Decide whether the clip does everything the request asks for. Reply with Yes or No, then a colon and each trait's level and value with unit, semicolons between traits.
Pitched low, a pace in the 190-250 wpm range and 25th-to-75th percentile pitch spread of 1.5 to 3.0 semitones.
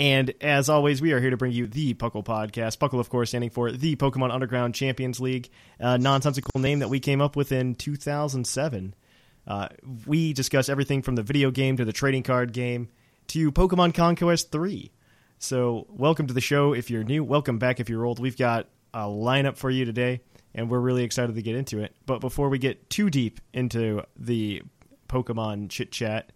Yes: low, 130 Hz; average, 200 wpm; average, 2.7 semitones